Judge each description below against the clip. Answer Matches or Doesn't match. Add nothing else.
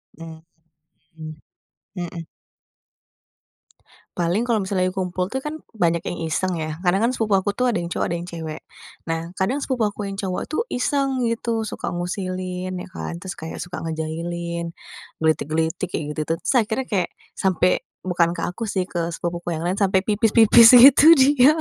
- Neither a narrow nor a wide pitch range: Matches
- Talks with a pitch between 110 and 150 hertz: Doesn't match